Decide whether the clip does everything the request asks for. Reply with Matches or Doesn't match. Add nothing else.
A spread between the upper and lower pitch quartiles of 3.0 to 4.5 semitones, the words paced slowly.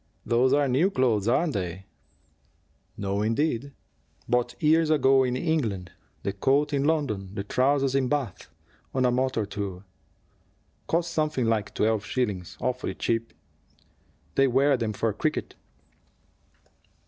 Doesn't match